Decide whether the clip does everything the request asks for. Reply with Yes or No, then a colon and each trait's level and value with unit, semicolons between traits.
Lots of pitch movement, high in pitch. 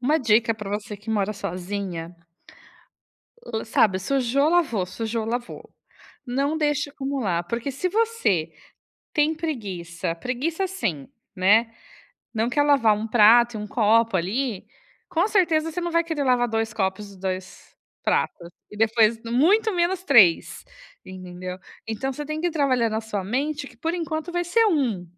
Yes: wide, 6.7 semitones; high, 235 Hz